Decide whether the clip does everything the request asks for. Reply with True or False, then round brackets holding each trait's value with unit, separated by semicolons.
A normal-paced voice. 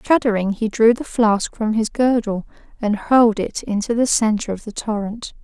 True (190 wpm)